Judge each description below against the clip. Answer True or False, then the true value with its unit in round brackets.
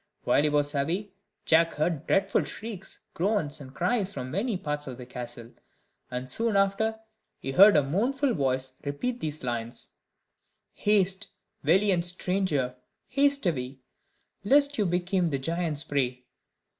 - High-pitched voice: False (165 Hz)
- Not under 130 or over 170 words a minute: True (140 wpm)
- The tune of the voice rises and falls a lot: True (6.6 semitones)